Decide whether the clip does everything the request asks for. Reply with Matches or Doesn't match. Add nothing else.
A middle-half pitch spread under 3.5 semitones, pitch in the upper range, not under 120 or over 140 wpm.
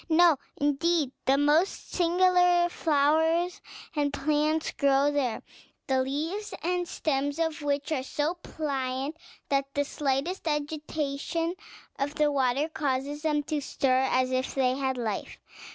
Matches